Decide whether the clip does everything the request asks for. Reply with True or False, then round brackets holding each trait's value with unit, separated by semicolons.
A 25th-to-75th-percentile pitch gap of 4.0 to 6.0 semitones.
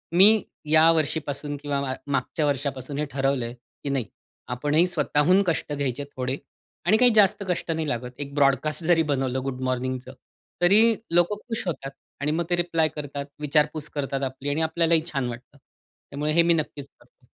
False (3.3 semitones)